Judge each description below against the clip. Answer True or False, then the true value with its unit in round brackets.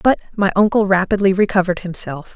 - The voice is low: False (190 Hz)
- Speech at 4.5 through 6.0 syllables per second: False (6.3 syllables/s)